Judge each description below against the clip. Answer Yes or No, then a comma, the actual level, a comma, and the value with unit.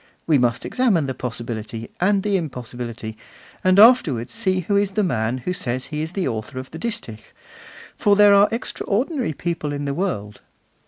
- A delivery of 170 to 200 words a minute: Yes, average, 175 wpm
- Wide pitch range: Yes, wide, 8.6 semitones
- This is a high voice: No, medium, 155 Hz